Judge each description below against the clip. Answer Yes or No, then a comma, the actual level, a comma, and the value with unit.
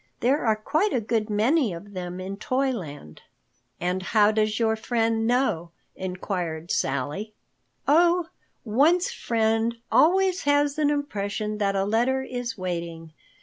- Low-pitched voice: No, high, 220 Hz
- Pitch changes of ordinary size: No, wide, 6.0 semitones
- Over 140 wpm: No, slow, 135 wpm